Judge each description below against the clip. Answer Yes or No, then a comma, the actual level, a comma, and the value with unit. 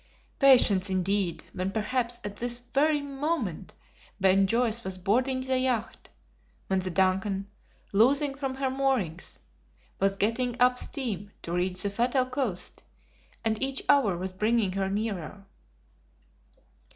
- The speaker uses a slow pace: Yes, slow, 130 wpm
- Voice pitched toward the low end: No, high, 220 Hz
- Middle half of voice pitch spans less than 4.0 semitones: No, average, 5.1 semitones